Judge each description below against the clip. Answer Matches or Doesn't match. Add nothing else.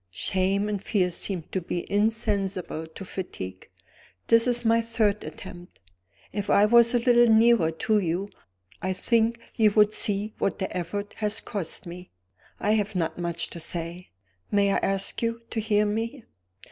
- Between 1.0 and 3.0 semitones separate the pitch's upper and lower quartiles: Doesn't match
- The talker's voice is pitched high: Matches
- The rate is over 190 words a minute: Doesn't match